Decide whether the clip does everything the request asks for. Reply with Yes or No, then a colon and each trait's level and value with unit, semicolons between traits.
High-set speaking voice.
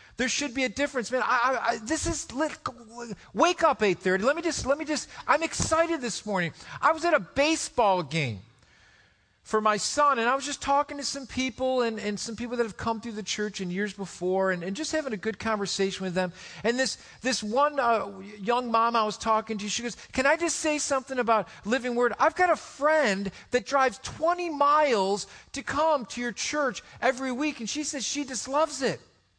Yes: high, 245 Hz